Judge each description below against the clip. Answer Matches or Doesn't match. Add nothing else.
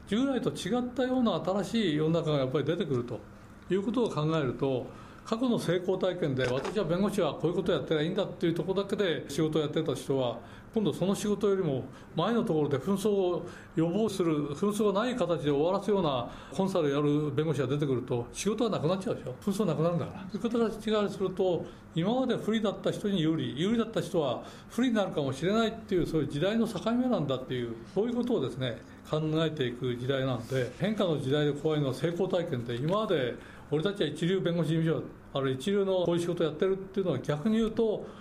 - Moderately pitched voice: Matches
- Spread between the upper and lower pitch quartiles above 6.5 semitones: Doesn't match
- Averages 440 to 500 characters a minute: Matches